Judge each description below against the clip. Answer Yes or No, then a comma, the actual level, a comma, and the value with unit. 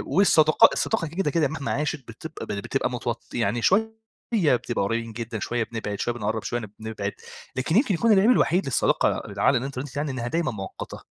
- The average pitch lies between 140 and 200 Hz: No, low, 130 Hz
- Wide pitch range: Yes, wide, 6.0 semitones